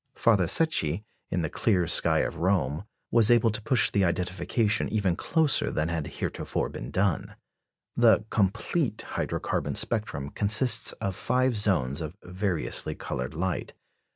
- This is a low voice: Yes, low, 100 Hz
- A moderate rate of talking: Yes, average, 145 wpm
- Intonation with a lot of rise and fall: No, average, 4.7 semitones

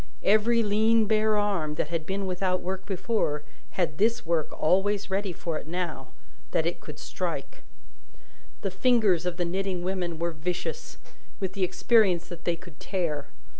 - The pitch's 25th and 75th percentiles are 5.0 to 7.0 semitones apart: No, average, 3.3 semitones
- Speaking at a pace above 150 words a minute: Yes, average, 165 wpm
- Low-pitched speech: No, medium, 185 Hz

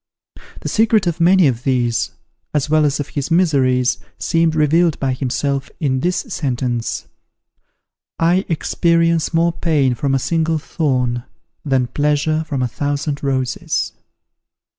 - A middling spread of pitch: Yes, average, 4.1 semitones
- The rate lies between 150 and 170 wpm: No, slow, 135 wpm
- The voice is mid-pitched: Yes, medium, 145 Hz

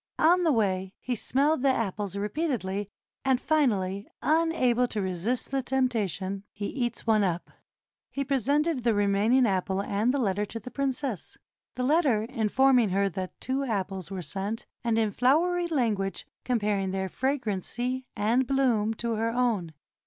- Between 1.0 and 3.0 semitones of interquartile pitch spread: No, average, 4.9 semitones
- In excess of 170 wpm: No, average, 160 wpm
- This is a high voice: Yes, high, 230 Hz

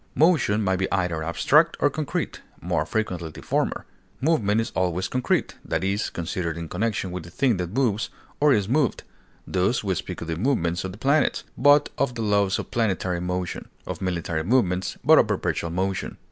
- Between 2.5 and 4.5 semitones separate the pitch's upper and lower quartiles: No, wide, 5.4 semitones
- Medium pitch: No, very low, 95 Hz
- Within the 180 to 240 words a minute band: Yes, average, 190 wpm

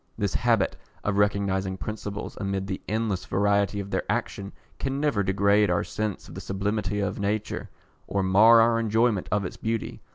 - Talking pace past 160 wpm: Yes, average, 170 wpm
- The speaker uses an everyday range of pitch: No, narrow, 1.8 semitones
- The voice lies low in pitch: Yes, low, 100 Hz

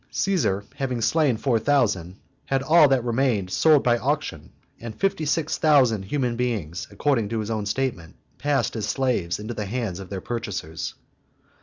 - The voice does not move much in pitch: No, average, 5.0 semitones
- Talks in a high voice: No, low, 120 Hz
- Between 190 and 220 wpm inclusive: No, average, 165 wpm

